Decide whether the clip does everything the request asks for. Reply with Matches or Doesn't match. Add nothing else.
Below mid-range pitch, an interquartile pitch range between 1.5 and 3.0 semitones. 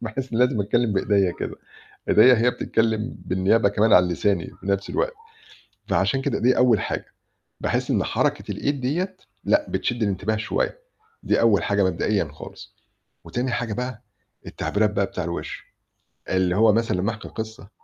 Doesn't match